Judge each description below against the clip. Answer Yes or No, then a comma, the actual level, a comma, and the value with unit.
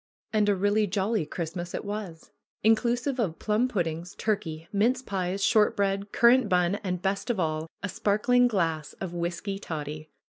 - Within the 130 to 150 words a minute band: No, average, 165 wpm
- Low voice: No, high, 195 Hz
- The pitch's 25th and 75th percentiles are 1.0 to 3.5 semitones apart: No, average, 3.9 semitones